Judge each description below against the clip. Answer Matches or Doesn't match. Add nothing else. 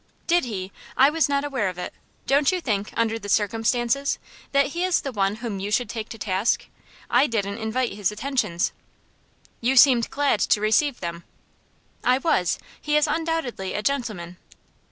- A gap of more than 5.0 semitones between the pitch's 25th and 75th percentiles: Matches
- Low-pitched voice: Doesn't match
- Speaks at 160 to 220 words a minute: Matches